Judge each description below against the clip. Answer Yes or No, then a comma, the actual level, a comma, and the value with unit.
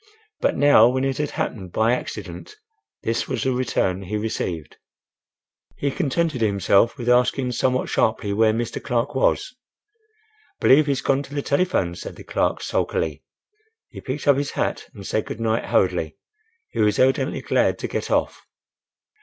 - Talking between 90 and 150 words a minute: No, average, 160 wpm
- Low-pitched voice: Yes, low, 125 Hz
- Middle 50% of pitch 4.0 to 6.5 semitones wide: Yes, average, 4.4 semitones